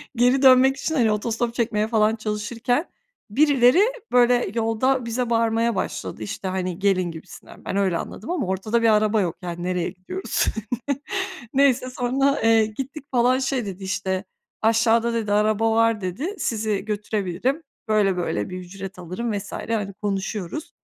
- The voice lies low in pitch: No, high, 220 Hz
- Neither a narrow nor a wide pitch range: Yes, average, 4.0 semitones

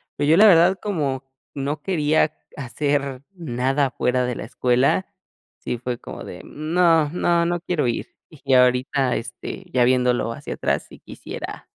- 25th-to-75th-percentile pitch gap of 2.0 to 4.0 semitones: No, average, 4.7 semitones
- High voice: No, medium, 140 Hz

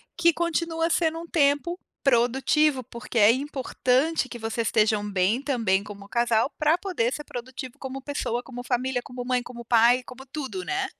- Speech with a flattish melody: No, average, 4.3 semitones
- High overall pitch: Yes, very high, 255 Hz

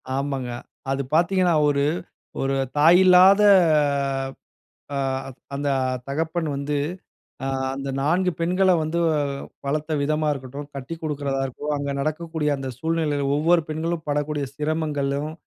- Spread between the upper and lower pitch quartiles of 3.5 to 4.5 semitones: No, average, 2.8 semitones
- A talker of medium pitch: Yes, medium, 150 Hz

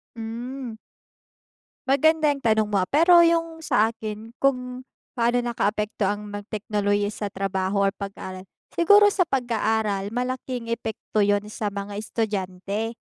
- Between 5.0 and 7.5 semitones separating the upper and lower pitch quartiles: No, average, 3.6 semitones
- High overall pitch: Yes, high, 220 Hz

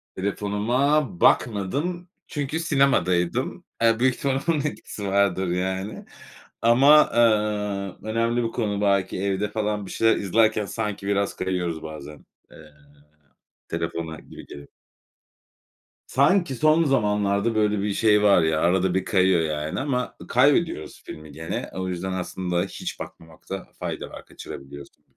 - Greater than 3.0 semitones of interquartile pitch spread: Yes, average, 4.2 semitones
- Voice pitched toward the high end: No, low, 100 Hz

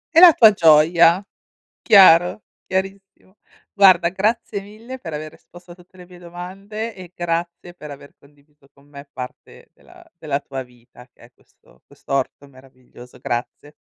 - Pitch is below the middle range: No, medium, 170 Hz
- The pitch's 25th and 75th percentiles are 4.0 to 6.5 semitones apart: Yes, average, 5.3 semitones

